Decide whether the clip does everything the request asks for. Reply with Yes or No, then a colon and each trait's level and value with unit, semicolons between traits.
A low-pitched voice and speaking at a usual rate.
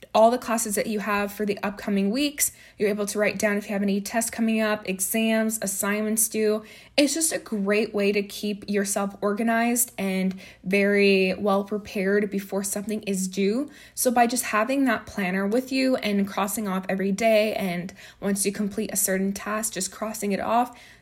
No: high, 205 Hz; average, 190 wpm